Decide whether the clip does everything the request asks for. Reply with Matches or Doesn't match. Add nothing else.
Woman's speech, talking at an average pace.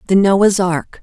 Matches